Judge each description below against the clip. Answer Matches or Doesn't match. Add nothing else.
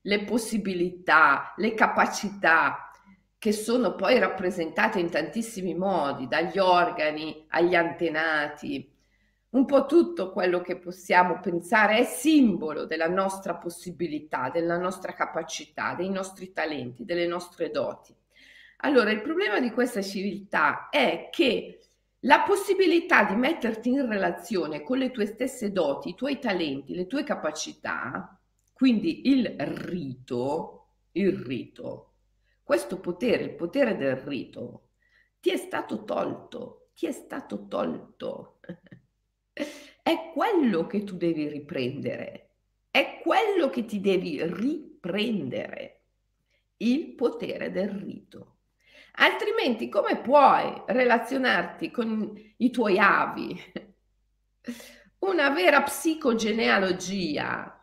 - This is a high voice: Matches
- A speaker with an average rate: Doesn't match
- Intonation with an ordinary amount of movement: Doesn't match